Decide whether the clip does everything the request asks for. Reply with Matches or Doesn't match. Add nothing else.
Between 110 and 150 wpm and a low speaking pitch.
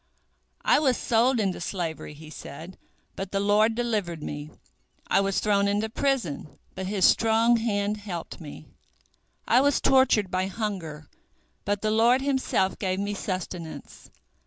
Doesn't match